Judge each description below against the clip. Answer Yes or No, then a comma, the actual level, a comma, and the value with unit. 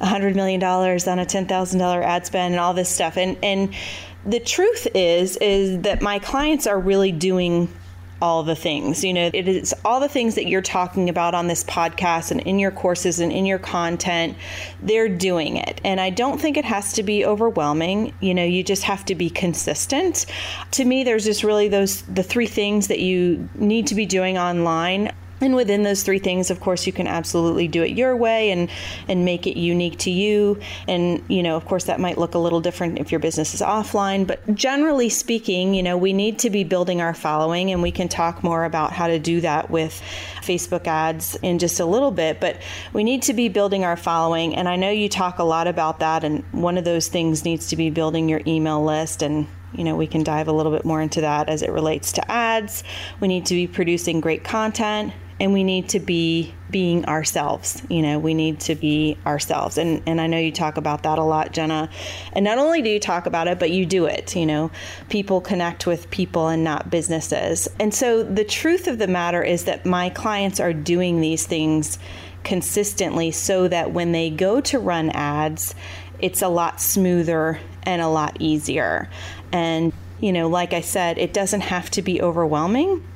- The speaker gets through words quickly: Yes, fast, 215 wpm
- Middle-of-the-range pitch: Yes, medium, 175 Hz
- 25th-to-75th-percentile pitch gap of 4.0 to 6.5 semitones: No, average, 3.3 semitones